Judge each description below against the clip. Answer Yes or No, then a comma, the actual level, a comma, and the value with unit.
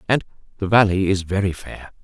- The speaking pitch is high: No, low, 100 Hz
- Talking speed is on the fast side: No, average, 175 wpm